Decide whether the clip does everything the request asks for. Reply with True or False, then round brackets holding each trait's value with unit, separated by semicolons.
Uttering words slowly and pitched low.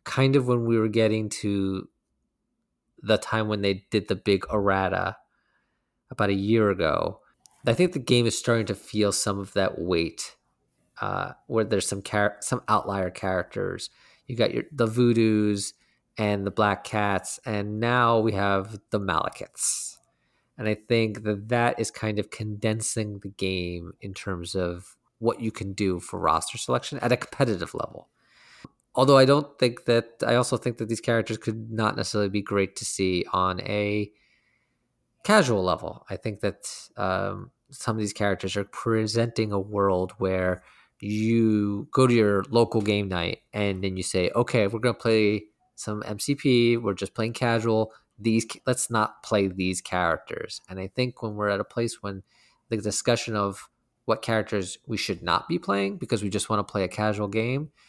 False (175 wpm; 105 Hz)